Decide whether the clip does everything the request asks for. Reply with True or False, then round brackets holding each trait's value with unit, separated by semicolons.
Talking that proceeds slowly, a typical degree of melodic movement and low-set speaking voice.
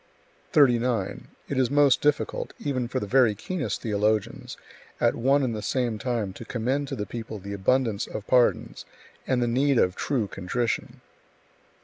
False (160 wpm; 3.7 semitones; 120 Hz)